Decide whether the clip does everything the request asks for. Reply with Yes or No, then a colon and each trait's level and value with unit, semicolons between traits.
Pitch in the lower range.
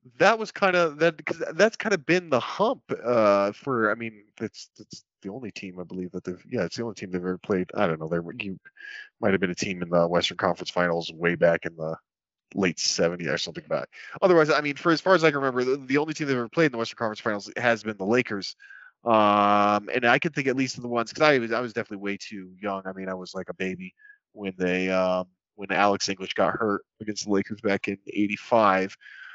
Yes: low, 105 Hz